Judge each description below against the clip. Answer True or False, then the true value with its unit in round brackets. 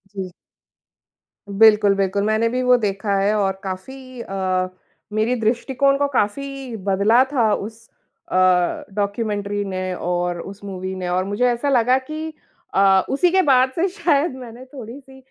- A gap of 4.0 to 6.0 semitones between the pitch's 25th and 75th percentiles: True (5.0 semitones)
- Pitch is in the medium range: False (220 Hz)